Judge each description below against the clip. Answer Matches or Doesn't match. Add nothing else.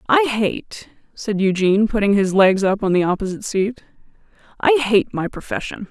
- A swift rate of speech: Doesn't match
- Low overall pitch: Doesn't match